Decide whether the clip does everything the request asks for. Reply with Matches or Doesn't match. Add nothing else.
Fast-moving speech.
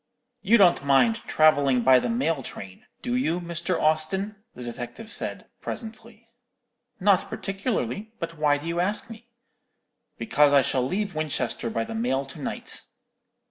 Doesn't match